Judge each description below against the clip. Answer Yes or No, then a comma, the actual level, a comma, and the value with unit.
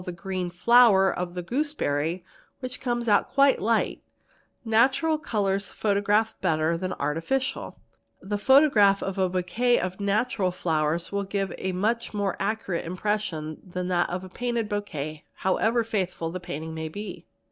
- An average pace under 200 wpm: Yes, average, 155 wpm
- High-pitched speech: Yes, high, 195 Hz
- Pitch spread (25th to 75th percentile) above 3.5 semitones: Yes, average, 4.1 semitones